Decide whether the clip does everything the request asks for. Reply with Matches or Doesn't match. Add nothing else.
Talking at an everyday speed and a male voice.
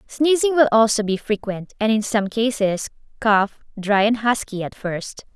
Doesn't match